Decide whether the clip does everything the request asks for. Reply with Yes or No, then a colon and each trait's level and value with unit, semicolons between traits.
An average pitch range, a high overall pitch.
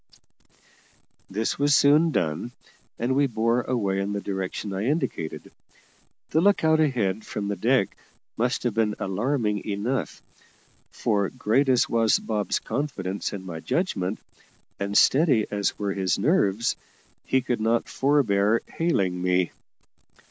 No: average, 5.0 semitones; low, 110 Hz